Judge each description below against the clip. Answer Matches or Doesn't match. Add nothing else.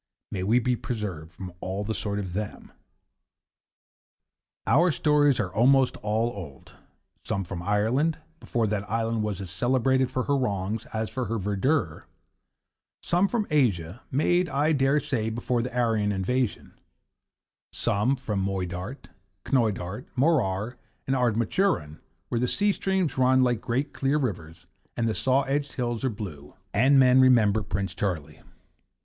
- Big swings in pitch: Doesn't match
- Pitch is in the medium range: Doesn't match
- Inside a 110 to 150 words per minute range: Matches